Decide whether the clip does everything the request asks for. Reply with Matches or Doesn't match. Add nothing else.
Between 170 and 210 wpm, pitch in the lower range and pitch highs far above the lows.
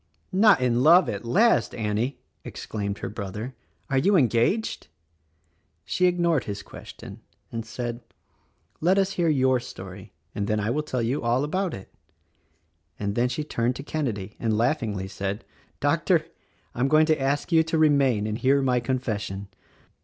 Doesn't match